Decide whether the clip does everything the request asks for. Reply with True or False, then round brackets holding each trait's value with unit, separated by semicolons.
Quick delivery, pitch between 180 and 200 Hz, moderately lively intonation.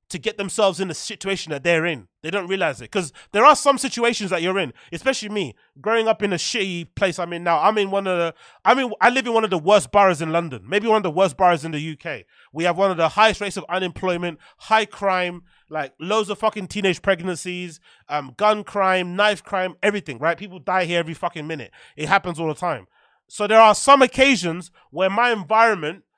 True (230 wpm; 190 Hz; 3.5 semitones)